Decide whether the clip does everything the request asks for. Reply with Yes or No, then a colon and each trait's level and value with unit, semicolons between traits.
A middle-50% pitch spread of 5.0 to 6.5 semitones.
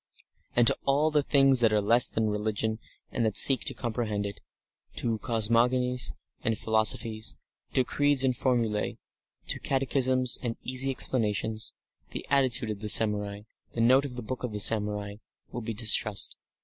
No: average, 3.0 semitones